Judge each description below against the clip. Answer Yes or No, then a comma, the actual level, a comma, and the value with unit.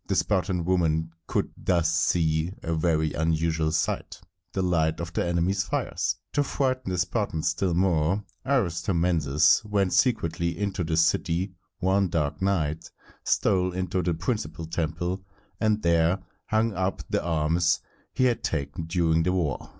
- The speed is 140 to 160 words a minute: Yes, average, 145 wpm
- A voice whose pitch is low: Yes, very low, 85 Hz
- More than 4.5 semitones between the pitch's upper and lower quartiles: No, average, 2.8 semitones